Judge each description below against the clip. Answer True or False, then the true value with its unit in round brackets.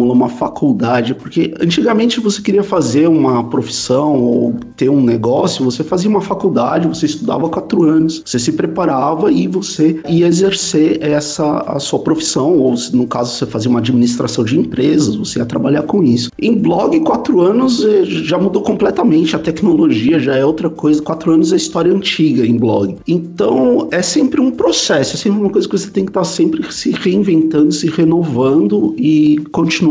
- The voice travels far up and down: True (5.7 semitones)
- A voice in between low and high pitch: True (160 Hz)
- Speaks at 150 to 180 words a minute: True (175 wpm)